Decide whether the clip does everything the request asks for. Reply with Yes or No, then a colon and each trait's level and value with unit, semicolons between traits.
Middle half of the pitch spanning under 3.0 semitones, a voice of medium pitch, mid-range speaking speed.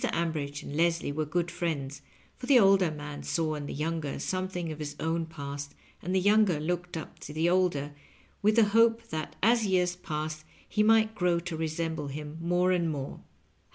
No: average, 3.4 semitones; medium, 165 Hz; average, 190 wpm